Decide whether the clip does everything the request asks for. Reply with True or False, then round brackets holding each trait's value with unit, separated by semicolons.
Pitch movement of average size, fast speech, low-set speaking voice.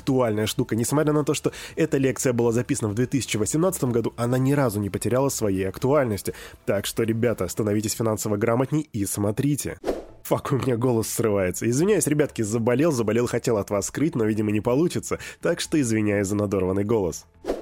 True (4.3 semitones; 175 wpm; 120 Hz)